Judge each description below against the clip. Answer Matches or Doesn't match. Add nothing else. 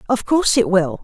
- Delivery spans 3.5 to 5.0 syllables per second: Doesn't match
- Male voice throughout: Doesn't match